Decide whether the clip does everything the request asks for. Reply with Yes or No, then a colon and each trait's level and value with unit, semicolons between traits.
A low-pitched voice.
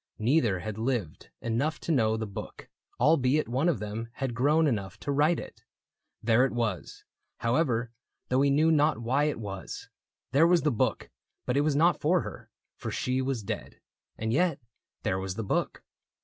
Yes: low, 125 Hz